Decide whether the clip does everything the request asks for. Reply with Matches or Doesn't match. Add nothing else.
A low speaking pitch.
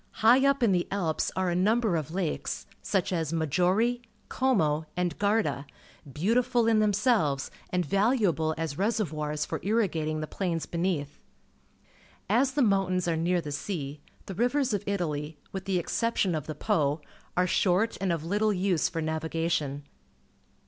Doesn't match